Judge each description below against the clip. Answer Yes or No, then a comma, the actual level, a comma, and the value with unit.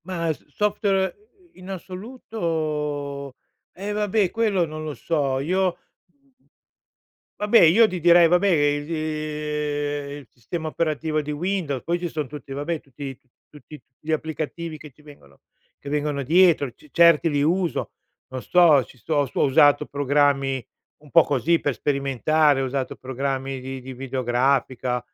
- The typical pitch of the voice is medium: Yes, medium, 150 Hz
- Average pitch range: Yes, average, 3.5 semitones